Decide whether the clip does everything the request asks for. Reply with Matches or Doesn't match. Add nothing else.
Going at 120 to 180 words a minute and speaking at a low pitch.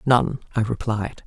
Matches